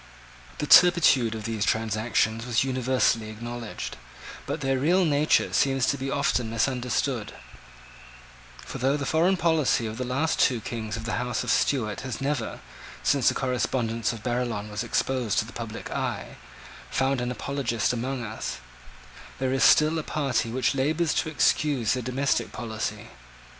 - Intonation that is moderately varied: Yes, average, 3.4 semitones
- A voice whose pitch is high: No, low, 125 Hz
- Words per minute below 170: Yes, average, 160 wpm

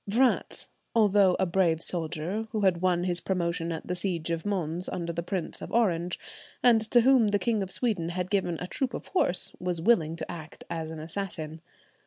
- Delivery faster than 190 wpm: Yes, average, 200 wpm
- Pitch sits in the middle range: Yes, medium, 180 Hz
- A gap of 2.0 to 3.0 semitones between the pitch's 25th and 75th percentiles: No, average, 3.4 semitones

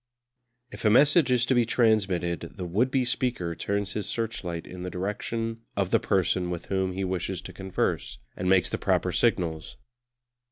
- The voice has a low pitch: Yes, very low, 95 Hz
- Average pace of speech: Yes, average, 175 wpm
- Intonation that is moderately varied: Yes, average, 4.2 semitones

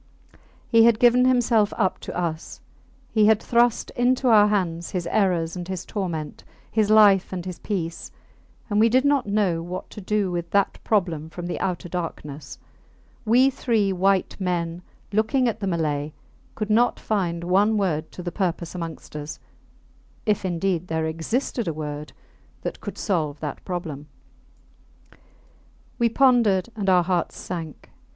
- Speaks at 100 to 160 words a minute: Yes, average, 155 wpm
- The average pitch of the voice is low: No, medium, 185 Hz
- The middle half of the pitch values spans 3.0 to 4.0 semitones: No, average, 4.4 semitones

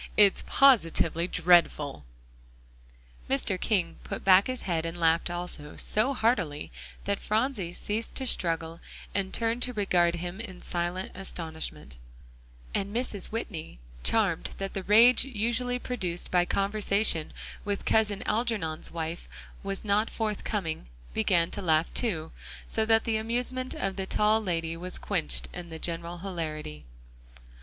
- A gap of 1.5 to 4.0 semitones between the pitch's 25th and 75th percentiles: No, average, 4.7 semitones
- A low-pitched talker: No, high, 190 Hz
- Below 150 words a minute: Yes, slow, 135 wpm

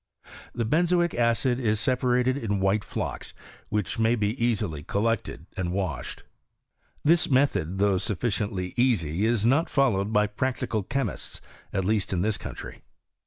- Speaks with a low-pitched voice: Yes, low, 110 Hz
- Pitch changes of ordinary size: Yes, average, 4.1 semitones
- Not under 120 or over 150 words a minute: Yes, average, 145 wpm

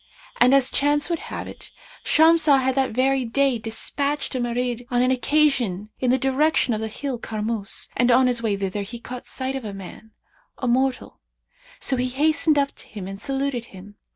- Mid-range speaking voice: No, very high, 250 Hz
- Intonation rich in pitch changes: No, average, 3.4 semitones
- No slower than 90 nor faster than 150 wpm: No, average, 195 wpm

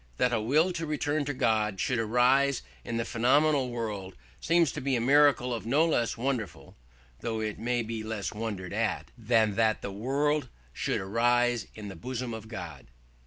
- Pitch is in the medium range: No, low, 120 Hz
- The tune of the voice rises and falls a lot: No, average, 3.7 semitones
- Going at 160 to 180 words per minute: Yes, average, 170 wpm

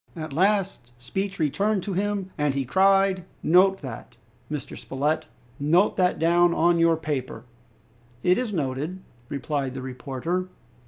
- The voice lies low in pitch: No, medium, 165 Hz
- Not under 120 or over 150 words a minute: Yes, average, 140 wpm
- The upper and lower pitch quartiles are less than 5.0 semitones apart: No, average, 5.3 semitones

